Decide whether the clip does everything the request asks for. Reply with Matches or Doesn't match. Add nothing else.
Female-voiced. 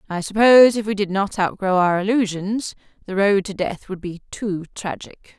Matches